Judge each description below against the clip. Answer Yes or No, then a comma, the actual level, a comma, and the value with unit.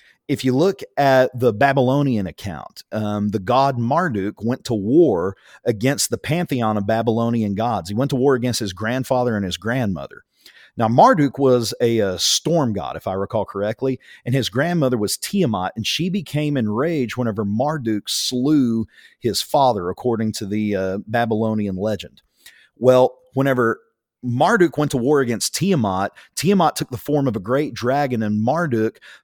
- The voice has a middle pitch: No, low, 120 Hz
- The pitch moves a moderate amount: Yes, average, 3.8 semitones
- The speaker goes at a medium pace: Yes, average, 160 wpm